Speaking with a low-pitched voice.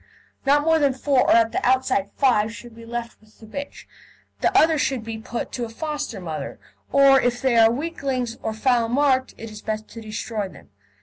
No: high, 240 Hz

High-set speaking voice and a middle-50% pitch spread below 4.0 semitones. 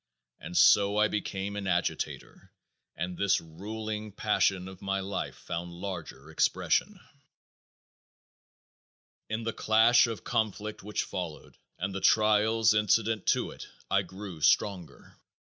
No: low, 100 Hz; narrow, 2.6 semitones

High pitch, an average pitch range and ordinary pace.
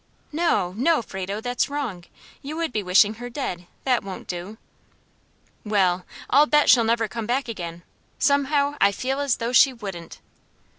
No: high, 230 Hz; wide, 6.2 semitones; average, 160 wpm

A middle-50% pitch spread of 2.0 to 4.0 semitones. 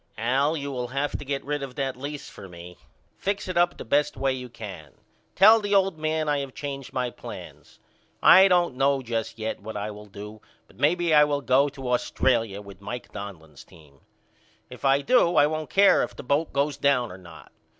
No: average, 5.1 semitones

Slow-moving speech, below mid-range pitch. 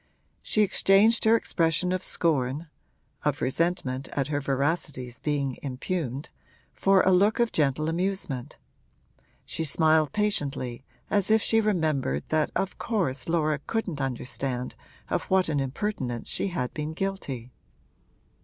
No: slow, 130 wpm; medium, 155 Hz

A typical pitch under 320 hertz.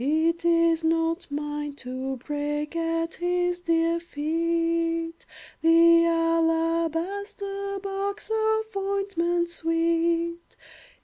No: very high, 335 Hz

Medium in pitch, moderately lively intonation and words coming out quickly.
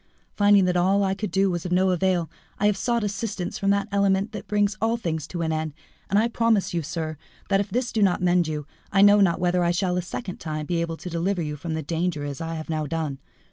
Yes: medium, 180 Hz; average, 3.5 semitones; fast, 255 wpm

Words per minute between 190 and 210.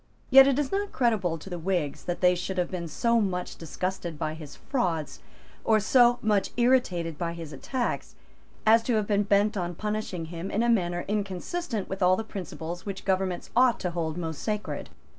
Yes: average, 195 wpm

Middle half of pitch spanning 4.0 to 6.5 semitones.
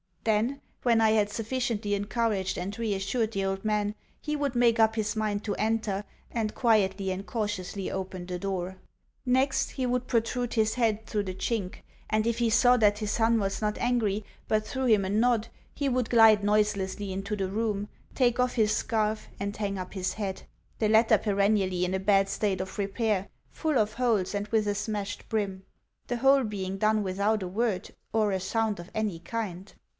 No: narrow, 2.6 semitones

